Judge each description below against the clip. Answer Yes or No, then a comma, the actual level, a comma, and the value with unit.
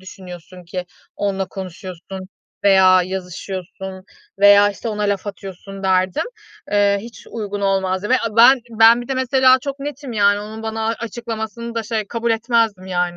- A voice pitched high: Yes, high, 205 Hz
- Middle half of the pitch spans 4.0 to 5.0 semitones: No, average, 3.4 semitones